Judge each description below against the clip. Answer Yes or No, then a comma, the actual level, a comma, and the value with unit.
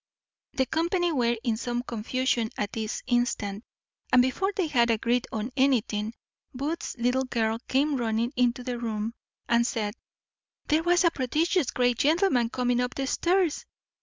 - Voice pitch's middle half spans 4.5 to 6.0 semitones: No, average, 3.4 semitones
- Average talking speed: Yes, average, 150 wpm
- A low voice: No, high, 245 Hz